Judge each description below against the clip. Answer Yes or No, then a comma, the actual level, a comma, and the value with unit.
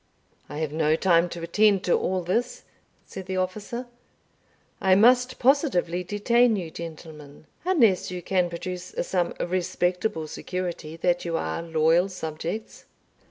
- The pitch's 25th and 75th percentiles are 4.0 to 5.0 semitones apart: No, average, 3.2 semitones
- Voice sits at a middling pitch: Yes, medium, 180 Hz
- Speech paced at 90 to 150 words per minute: Yes, slow, 135 wpm